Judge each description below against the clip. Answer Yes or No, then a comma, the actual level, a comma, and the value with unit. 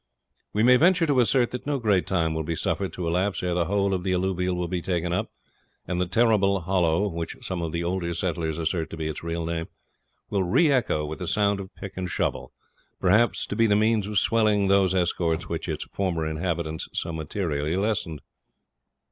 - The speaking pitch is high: No, very low, 90 Hz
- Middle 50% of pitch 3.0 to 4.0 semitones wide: Yes, average, 3.4 semitones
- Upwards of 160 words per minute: Yes, fast, 205 wpm